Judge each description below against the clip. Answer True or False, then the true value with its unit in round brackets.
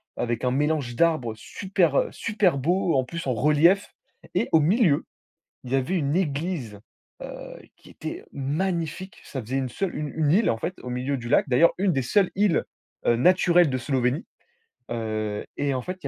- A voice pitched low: False (145 Hz)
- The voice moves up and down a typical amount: False (5.9 semitones)